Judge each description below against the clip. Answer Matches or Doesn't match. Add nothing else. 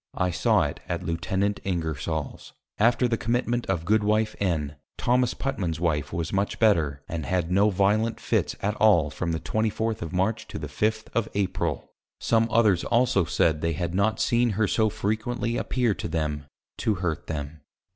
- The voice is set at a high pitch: Doesn't match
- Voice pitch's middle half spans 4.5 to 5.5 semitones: Matches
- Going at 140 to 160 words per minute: Doesn't match